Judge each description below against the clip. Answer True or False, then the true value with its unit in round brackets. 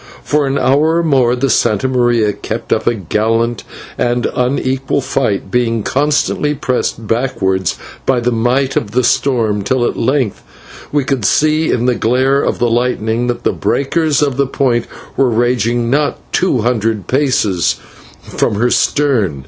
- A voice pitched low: True (125 Hz)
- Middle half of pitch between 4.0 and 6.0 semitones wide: False (3.1 semitones)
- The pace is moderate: True (160 wpm)